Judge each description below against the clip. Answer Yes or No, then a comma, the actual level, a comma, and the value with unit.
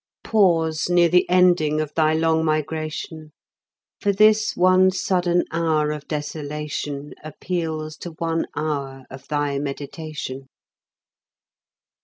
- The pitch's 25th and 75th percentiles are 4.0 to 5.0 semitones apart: No, average, 2.7 semitones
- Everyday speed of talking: No, slow, 110 wpm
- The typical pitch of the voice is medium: Yes, medium, 155 Hz